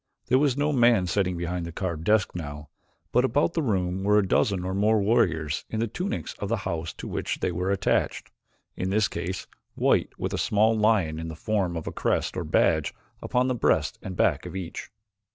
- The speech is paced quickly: Yes, fast, 210 wpm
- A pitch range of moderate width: Yes, average, 4.3 semitones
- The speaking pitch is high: No, very low, 95 Hz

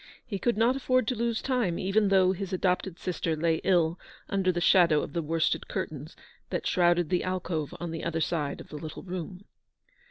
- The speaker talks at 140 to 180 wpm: No, average, 195 wpm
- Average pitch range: Yes, average, 3.1 semitones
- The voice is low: No, medium, 180 Hz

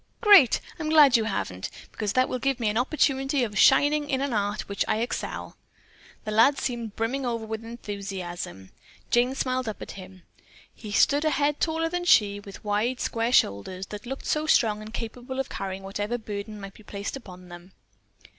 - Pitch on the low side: No, high, 225 Hz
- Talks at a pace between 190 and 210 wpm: Yes, average, 195 wpm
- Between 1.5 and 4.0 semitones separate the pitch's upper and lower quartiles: No, average, 4.8 semitones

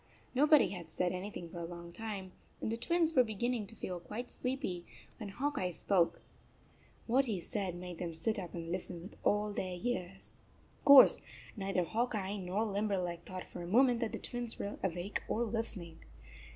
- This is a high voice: Yes, high, 200 Hz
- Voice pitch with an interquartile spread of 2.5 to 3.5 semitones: No, average, 4.5 semitones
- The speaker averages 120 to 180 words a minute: No, average, 190 wpm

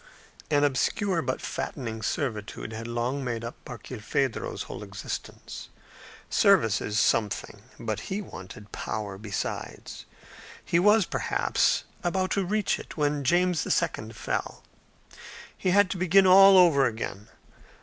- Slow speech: Yes, slow, 130 wpm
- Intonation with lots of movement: Yes, wide, 8.5 semitones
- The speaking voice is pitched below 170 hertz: Yes, medium, 140 Hz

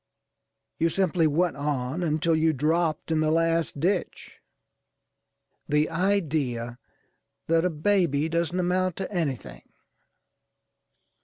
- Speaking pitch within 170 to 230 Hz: No, medium, 160 Hz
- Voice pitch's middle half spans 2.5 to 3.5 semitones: Yes, average, 2.9 semitones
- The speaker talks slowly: Yes, slow, 105 wpm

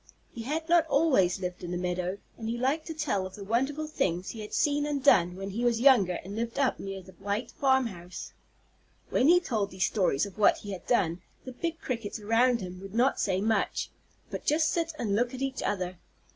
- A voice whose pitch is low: No, high, 225 Hz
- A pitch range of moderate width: No, wide, 6.3 semitones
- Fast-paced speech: Yes, fast, 225 wpm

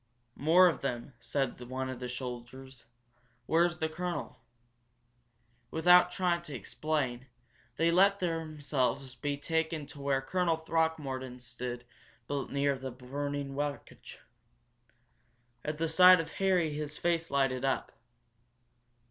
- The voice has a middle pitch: Yes, medium, 145 Hz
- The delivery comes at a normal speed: No, slow, 120 wpm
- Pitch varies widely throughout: No, average, 3.8 semitones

